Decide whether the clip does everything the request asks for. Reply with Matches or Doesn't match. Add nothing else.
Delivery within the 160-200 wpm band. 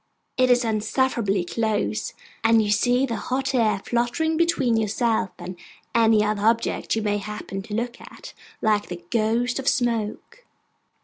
Doesn't match